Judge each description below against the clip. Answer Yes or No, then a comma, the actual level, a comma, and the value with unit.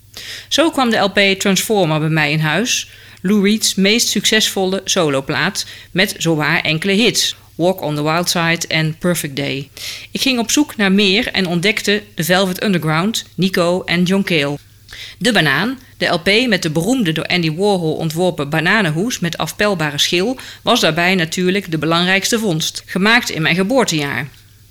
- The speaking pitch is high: No, medium, 180 Hz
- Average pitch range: Yes, average, 4.4 semitones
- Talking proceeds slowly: No, average, 160 wpm